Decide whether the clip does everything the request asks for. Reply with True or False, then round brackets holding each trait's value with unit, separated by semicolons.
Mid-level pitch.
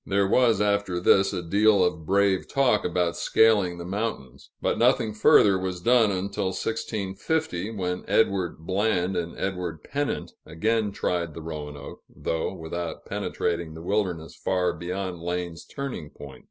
False (95 Hz)